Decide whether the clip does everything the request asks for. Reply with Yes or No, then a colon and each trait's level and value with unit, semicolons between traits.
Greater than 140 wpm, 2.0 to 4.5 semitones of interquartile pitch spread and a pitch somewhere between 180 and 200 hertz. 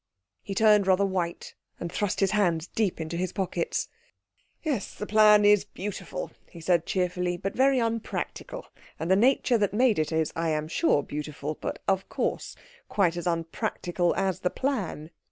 Yes: average, 170 wpm; average, 3.7 semitones; medium, 185 Hz